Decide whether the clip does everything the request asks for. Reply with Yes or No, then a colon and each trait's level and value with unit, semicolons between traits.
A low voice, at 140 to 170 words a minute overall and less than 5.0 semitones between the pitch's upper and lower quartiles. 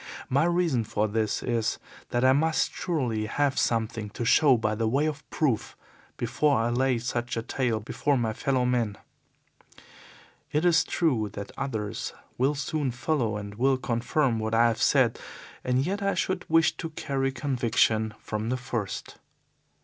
Yes: low, 125 Hz; average, 160 wpm; average, 4.0 semitones